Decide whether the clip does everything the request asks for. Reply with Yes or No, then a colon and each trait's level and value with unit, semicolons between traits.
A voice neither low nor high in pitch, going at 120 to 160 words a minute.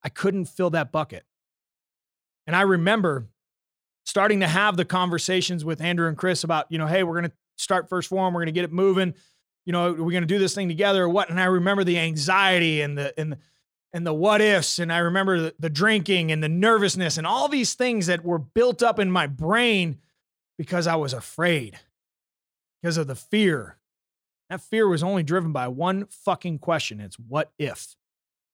No: medium, 175 Hz; average, 200 wpm